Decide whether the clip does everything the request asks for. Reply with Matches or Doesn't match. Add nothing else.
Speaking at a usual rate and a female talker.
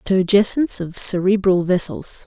Doesn't match